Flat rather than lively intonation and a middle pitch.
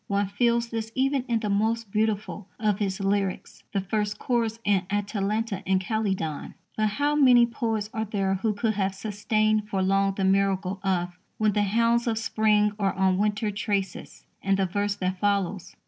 No: narrow, 2.1 semitones; high, 205 Hz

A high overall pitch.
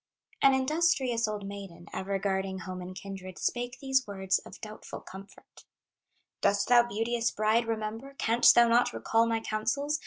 Yes: high, 220 Hz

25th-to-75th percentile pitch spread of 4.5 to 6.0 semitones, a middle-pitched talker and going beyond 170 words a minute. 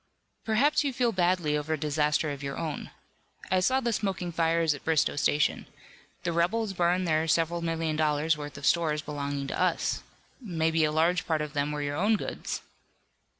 No: average, 3.3 semitones; medium, 160 Hz; average, 185 wpm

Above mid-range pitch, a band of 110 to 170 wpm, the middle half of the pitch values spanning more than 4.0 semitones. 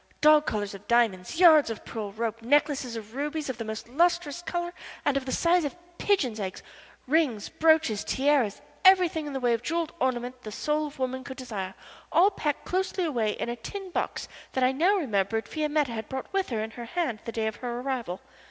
No: very high, 260 Hz; fast, 205 wpm; wide, 5.6 semitones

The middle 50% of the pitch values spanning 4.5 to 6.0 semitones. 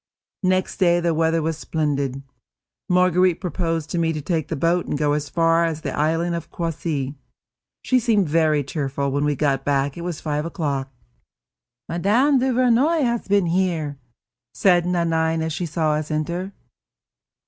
No: average, 3.2 semitones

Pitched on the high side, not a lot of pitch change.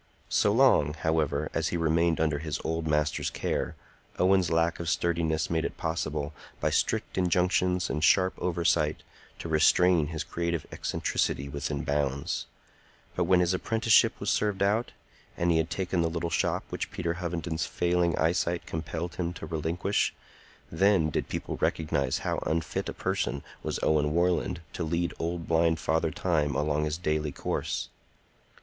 No: very low, 85 Hz; narrow, 2.2 semitones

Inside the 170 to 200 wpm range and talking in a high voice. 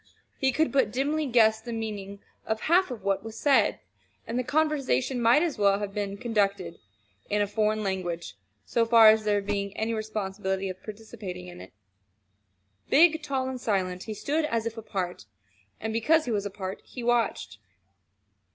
Yes: average, 175 wpm; high, 220 Hz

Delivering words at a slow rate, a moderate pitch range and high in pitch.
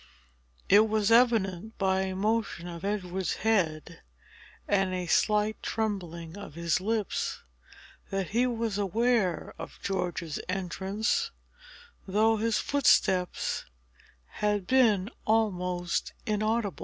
Yes: slow, 105 wpm; average, 3.3 semitones; high, 200 Hz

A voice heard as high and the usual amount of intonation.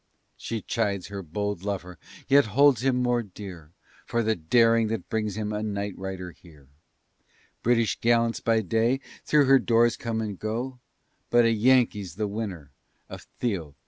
No: low, 110 Hz; average, 3.2 semitones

